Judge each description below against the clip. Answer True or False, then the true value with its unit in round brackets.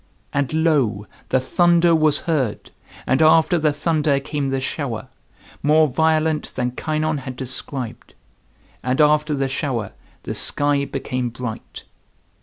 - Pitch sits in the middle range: True (145 Hz)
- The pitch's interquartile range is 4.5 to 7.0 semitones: False (3.3 semitones)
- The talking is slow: True (130 wpm)